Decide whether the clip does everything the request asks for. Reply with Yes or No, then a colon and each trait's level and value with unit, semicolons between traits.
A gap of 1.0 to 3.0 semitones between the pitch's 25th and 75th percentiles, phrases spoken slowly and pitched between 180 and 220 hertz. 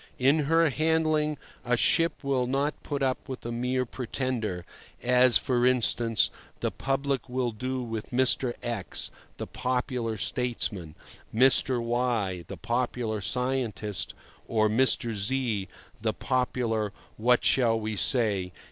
No: average, 2.7 semitones; slow, 125 wpm; low, 125 Hz